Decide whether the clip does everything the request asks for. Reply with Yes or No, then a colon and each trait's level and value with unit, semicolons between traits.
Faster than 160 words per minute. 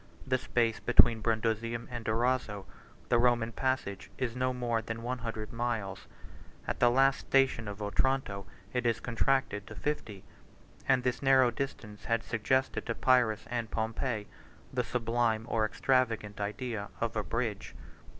No: average, 155 wpm